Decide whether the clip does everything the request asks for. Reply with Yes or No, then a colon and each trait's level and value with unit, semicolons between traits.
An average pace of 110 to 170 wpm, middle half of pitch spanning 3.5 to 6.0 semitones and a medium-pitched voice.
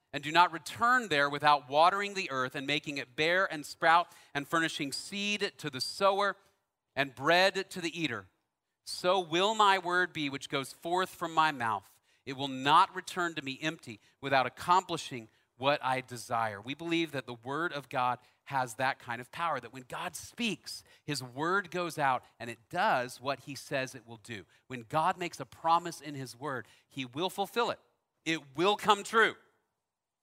No: average, 185 wpm; average, 5.2 semitones; medium, 150 Hz